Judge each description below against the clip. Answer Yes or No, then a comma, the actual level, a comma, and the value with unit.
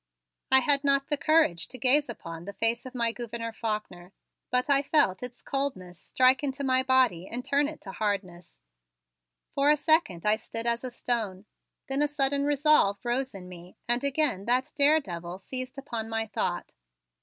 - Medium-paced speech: Yes, average, 180 wpm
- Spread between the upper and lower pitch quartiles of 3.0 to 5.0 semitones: No, wide, 5.5 semitones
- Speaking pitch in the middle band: No, high, 245 Hz